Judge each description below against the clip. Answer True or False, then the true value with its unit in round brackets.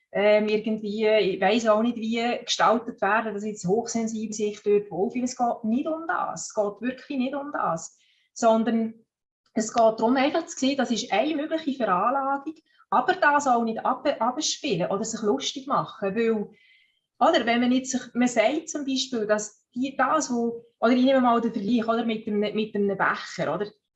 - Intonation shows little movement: False (3.7 semitones)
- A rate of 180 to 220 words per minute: True (190 wpm)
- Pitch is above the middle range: True (230 Hz)